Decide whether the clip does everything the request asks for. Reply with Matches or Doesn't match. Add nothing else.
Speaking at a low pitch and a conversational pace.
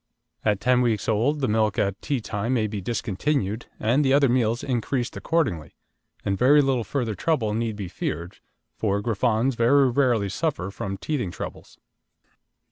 Matches